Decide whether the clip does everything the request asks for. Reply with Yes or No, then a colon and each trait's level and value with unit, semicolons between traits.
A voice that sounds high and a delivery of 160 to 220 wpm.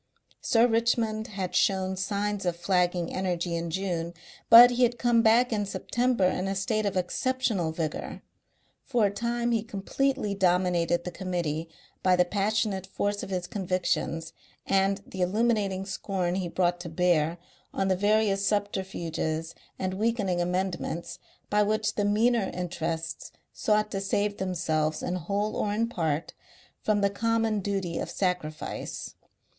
No: high, 195 Hz; average, 150 wpm